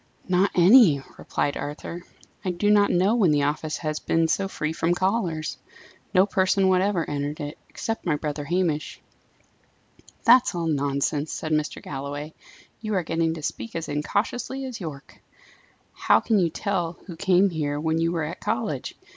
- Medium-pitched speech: Yes, medium, 165 Hz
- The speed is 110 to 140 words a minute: No, average, 165 wpm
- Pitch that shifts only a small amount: No, average, 4.2 semitones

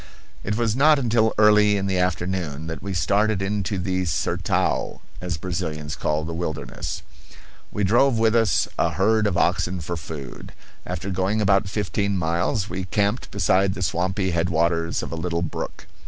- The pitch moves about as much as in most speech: Yes, average, 3.6 semitones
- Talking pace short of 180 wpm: Yes, average, 165 wpm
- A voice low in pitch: Yes, very low, 95 Hz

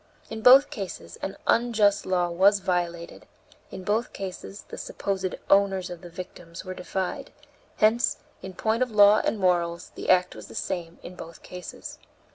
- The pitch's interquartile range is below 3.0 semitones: Yes, narrow, 2.6 semitones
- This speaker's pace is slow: No, average, 165 wpm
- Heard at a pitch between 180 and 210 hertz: Yes, high, 190 Hz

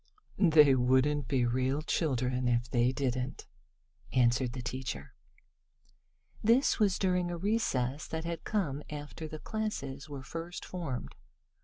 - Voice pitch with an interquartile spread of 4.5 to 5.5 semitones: Yes, average, 4.9 semitones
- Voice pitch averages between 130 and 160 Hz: Yes, medium, 140 Hz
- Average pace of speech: No, slow, 130 wpm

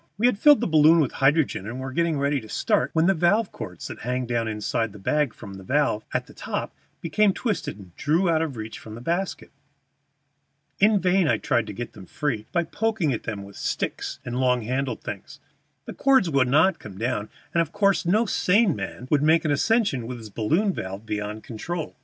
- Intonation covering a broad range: Yes, wide, 7.5 semitones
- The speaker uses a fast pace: Yes, fast, 220 wpm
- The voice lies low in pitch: No, medium, 145 Hz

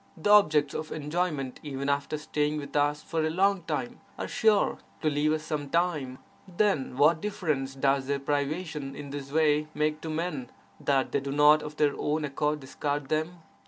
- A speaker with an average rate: Yes, average, 180 wpm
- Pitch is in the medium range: Yes, medium, 150 Hz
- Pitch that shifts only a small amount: Yes, narrow, 2.0 semitones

